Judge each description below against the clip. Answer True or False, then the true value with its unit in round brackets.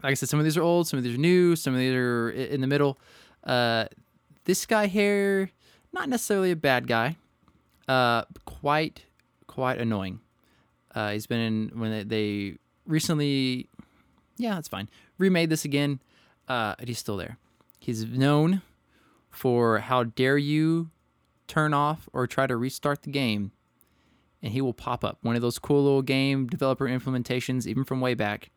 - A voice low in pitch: True (130 Hz)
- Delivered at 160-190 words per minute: True (175 wpm)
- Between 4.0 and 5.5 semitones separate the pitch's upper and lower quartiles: True (4.4 semitones)